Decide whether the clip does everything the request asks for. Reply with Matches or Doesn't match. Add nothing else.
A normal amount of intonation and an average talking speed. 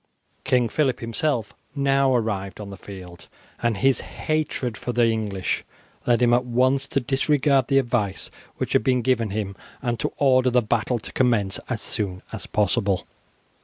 Matches